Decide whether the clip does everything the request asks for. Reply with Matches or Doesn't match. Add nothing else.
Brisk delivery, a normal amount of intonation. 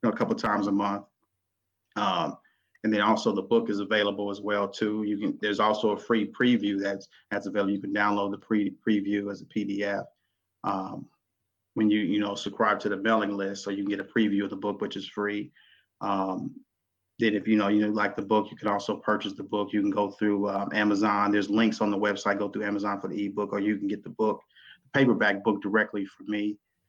Doesn't match